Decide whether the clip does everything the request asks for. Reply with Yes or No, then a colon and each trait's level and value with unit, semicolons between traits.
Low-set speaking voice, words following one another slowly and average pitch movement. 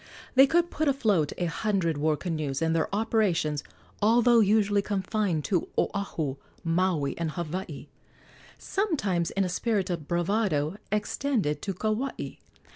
No: high, 190 Hz; slow, 130 wpm; average, 5.0 semitones